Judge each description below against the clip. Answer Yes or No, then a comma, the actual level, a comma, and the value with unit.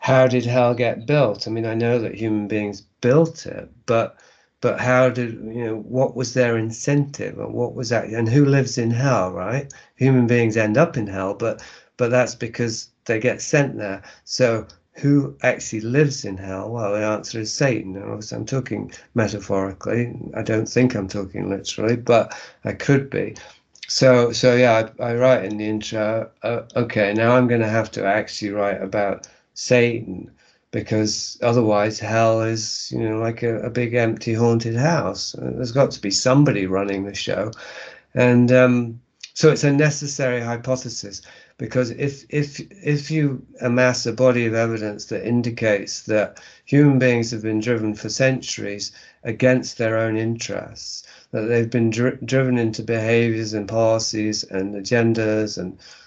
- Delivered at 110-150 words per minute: No, average, 170 wpm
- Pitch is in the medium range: No, low, 115 Hz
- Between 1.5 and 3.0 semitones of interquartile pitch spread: Yes, average, 2.7 semitones